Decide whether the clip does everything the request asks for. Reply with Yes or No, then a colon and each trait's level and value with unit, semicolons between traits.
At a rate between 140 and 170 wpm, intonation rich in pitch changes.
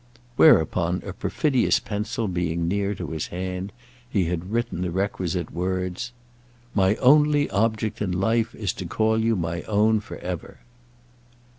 No: average, 145 wpm; average, 3.7 semitones